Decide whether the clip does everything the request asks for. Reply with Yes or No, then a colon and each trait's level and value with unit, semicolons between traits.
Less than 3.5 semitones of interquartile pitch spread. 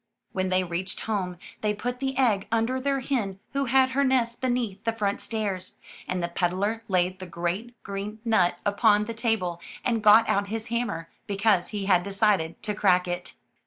No: average, 3.9 semitones